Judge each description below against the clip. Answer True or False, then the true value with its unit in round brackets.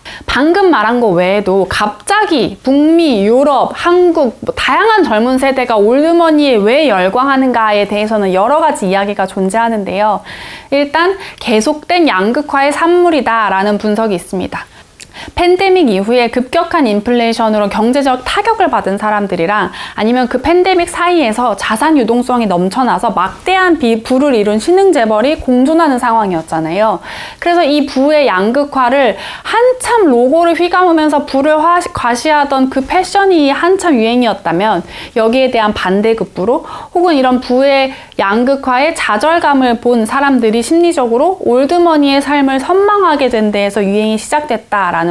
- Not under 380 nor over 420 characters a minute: False (330 characters per minute)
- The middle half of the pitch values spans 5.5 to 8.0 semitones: True (6.8 semitones)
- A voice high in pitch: True (260 Hz)